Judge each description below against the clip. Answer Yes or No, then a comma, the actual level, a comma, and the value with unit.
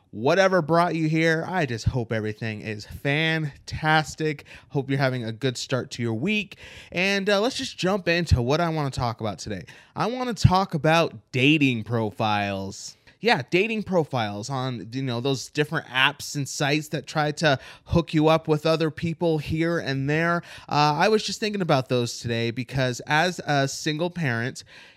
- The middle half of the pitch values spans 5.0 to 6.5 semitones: Yes, wide, 5.4 semitones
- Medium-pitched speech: Yes, medium, 150 Hz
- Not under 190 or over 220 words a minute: No, average, 180 wpm